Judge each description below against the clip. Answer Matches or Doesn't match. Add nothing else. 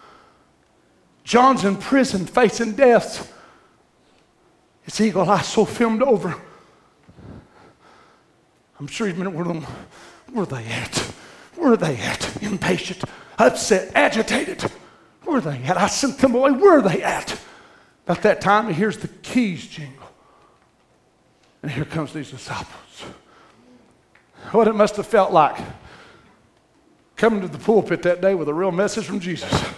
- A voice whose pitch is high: Matches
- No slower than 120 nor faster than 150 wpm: Matches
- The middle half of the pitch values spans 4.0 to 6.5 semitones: Matches